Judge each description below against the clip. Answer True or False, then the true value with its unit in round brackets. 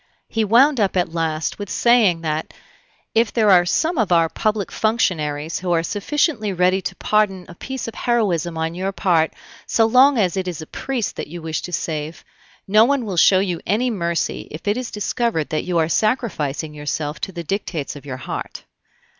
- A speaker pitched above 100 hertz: True (185 Hz)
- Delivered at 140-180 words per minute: False (195 wpm)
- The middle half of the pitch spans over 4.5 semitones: True (5.2 semitones)